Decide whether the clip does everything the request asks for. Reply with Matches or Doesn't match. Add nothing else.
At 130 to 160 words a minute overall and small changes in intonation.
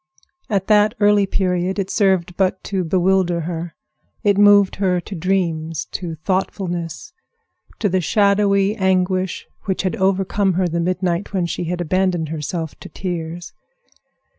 Matches